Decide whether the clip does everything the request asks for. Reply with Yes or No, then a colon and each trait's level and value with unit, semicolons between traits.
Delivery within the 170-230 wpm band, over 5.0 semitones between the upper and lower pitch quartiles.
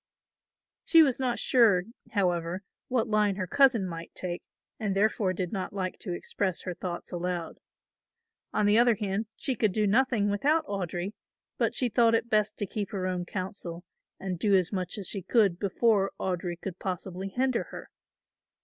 No: average, 175 wpm; average, 3.4 semitones